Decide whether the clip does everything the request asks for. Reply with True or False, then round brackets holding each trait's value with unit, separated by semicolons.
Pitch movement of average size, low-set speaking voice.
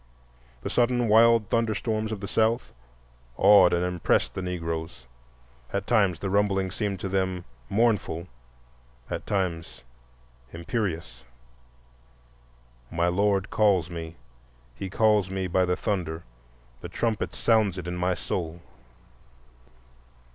True (3.6 semitones; 95 Hz)